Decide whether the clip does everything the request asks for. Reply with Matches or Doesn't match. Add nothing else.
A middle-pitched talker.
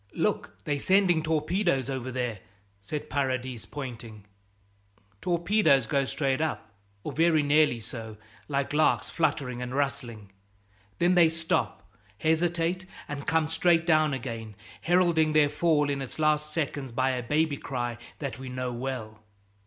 Matches